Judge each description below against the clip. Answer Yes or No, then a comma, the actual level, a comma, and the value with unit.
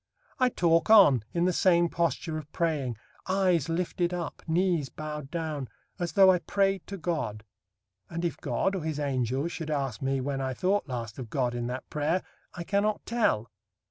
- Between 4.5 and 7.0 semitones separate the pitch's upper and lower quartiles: Yes, average, 5.0 semitones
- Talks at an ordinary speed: Yes, average, 180 wpm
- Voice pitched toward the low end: No, medium, 160 Hz